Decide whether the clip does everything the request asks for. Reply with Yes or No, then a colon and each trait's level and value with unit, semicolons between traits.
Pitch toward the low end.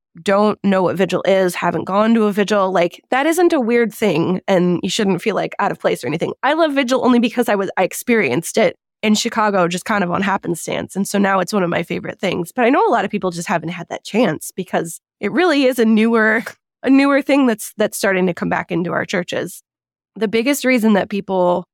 No: high, 200 Hz